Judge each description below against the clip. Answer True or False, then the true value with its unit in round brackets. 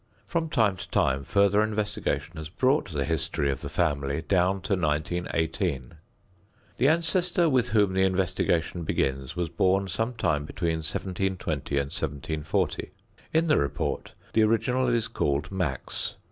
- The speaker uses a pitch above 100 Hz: False (90 Hz)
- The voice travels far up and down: True (6.2 semitones)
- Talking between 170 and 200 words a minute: False (145 wpm)